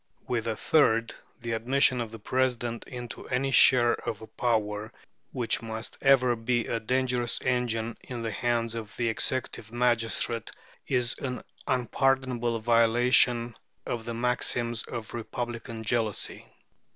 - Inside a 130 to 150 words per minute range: Yes, slow, 135 wpm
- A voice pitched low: Yes, low, 120 Hz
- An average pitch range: No, narrow, 1.6 semitones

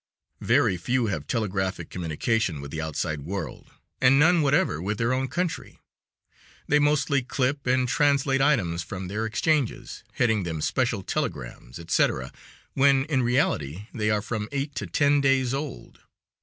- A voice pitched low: Yes, low, 120 Hz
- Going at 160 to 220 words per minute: No, average, 150 wpm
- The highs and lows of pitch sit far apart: Yes, wide, 7.0 semitones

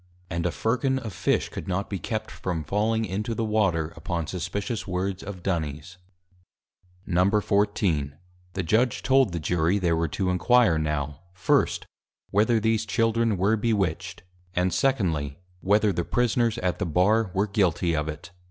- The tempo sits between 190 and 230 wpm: No, average, 155 wpm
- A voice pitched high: No, very low, 95 Hz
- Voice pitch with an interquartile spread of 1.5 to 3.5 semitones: No, average, 4.3 semitones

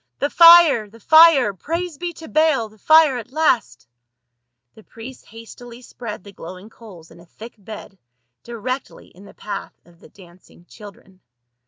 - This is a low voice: No, high, 225 Hz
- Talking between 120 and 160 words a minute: No, average, 170 wpm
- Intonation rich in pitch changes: Yes, wide, 6.9 semitones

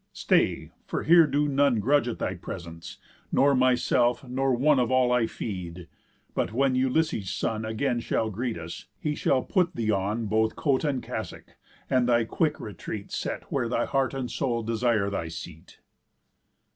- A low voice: Yes, low, 120 Hz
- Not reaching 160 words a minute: No, average, 170 wpm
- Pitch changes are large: No, average, 4.0 semitones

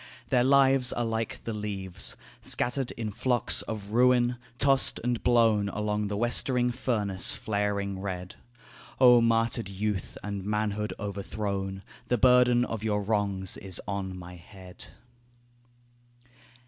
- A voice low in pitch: Yes, low, 105 Hz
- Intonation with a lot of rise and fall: No, average, 3.4 semitones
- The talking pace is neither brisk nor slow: No, slow, 125 wpm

